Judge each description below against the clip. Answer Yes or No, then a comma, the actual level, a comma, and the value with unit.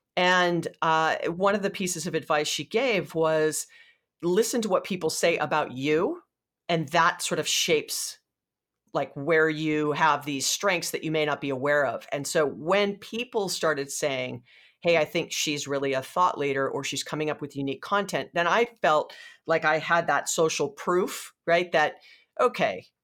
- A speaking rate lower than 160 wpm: No, average, 180 wpm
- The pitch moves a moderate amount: Yes, average, 3.7 semitones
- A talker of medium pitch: Yes, medium, 160 Hz